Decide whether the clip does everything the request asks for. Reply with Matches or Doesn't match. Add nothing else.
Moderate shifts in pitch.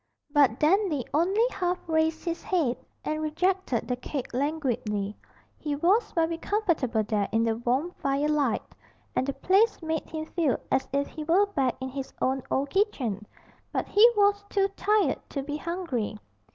Doesn't match